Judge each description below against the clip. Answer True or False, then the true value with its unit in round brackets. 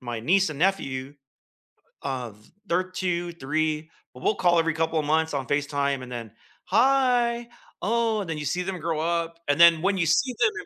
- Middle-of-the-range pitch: True (165 Hz)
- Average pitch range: True (4.8 semitones)